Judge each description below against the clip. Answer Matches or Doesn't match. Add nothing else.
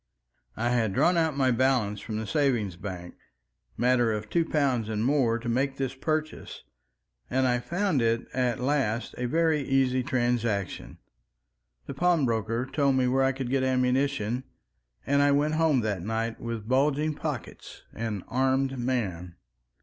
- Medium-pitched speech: Doesn't match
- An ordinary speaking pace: Matches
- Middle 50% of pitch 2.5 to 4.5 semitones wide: Matches